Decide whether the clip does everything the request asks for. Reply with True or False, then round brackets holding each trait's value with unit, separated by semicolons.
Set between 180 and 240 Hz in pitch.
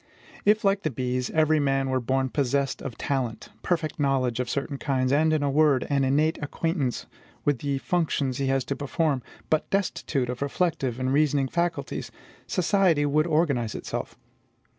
False (140 Hz)